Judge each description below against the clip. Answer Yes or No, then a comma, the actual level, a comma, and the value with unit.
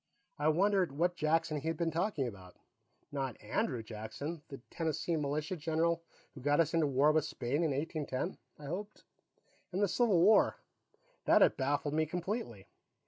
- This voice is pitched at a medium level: Yes, medium, 155 Hz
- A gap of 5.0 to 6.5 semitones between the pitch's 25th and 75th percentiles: No, average, 3.4 semitones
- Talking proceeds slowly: No, average, 165 wpm